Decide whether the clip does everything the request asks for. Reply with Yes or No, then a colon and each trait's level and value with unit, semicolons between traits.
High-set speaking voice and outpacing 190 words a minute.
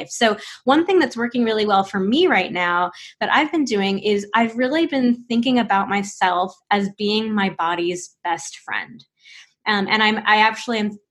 No: high, 210 Hz; average, 185 wpm